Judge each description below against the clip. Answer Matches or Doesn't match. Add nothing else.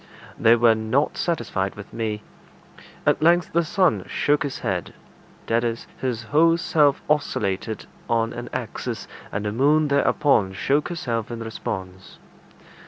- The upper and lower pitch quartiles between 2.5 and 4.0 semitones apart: Doesn't match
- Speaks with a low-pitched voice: Matches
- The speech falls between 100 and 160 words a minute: Matches